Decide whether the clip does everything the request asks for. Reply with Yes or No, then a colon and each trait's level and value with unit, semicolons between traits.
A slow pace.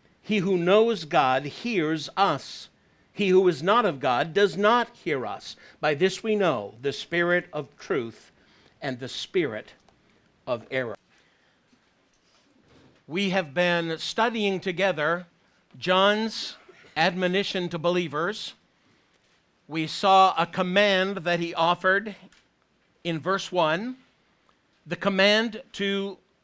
Yes: slow, 115 wpm